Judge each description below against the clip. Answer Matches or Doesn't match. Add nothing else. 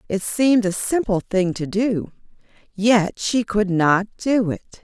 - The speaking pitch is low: Doesn't match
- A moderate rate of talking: Matches